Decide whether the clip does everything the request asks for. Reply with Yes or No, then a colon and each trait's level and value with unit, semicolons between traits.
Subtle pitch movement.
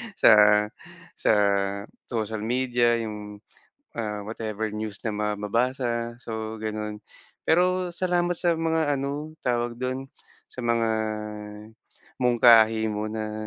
No: average, 3.3 semitones